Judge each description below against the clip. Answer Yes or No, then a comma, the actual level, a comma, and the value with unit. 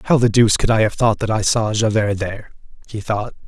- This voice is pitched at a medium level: No, low, 110 Hz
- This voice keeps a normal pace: No, fast, 240 wpm